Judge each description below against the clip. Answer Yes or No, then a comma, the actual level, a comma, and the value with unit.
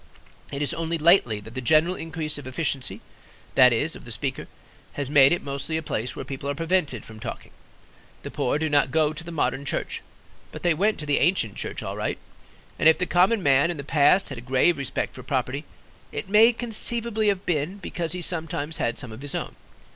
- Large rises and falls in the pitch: No, average, 4.4 semitones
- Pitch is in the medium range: Yes, medium, 150 Hz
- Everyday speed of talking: No, fast, 215 wpm